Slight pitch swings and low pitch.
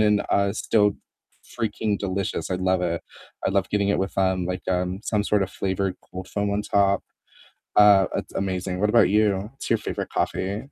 Yes: narrow, 1.8 semitones; low, 100 Hz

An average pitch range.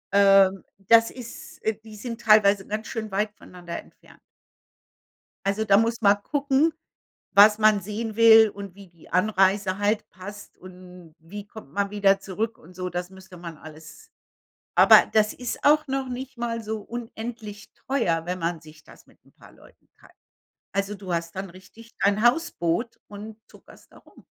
Yes: average, 3.3 semitones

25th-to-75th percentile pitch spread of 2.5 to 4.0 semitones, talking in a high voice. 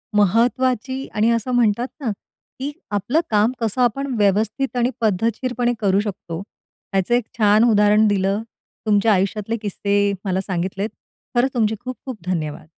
Yes: average, 3.3 semitones; high, 215 Hz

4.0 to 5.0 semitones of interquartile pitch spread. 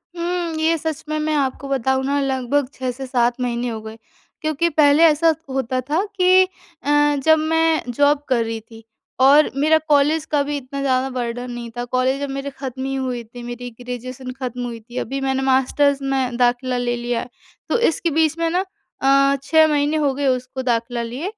No: average, 3.5 semitones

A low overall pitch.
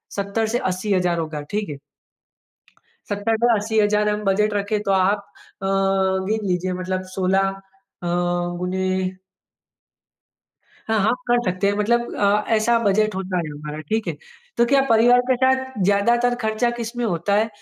No: high, 205 Hz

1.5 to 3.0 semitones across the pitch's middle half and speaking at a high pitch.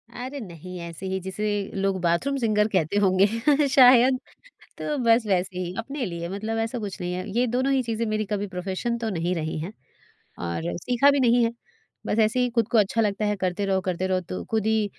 No: average, 4.3 semitones; high, 210 Hz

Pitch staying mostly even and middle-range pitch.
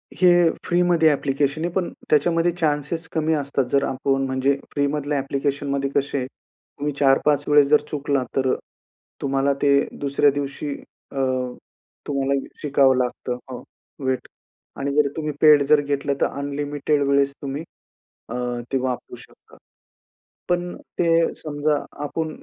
Yes: narrow, 1.7 semitones; medium, 145 Hz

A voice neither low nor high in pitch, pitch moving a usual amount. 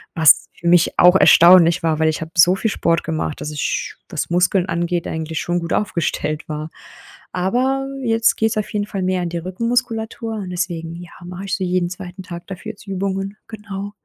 Yes: medium, 180 Hz; average, 3.1 semitones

